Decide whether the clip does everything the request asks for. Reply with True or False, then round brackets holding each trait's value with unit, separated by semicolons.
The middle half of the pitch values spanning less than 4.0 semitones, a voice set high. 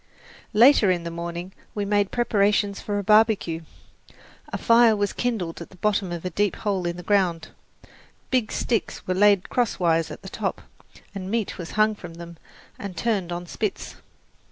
True (3.5 semitones; 200 Hz)